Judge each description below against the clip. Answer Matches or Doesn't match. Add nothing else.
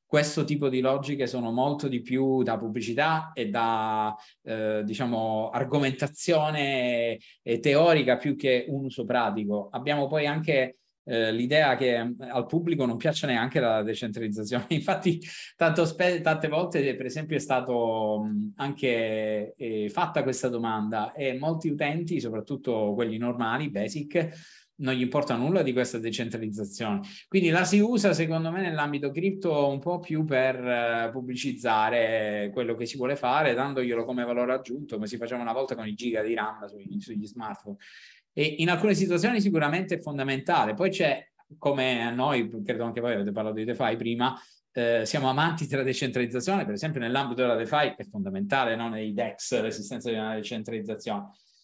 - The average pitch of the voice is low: Matches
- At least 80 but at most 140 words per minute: Doesn't match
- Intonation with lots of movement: Doesn't match